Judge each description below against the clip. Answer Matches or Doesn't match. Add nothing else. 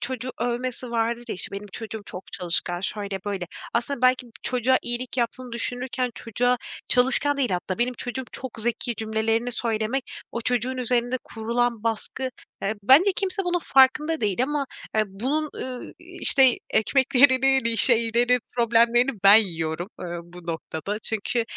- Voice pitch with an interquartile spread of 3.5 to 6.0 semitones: Doesn't match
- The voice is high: Matches